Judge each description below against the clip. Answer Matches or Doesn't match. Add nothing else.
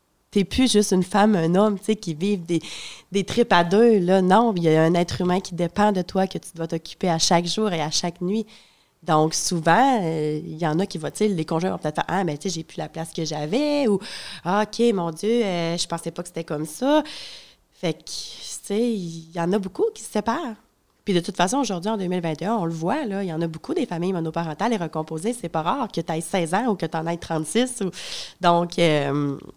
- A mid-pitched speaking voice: Matches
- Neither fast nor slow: Doesn't match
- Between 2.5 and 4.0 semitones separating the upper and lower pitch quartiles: Doesn't match